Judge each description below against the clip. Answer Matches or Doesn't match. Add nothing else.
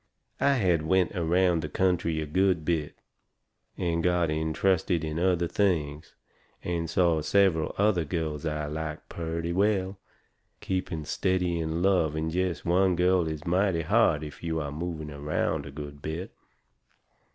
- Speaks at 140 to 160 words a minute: Matches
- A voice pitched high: Doesn't match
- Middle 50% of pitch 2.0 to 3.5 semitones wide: Matches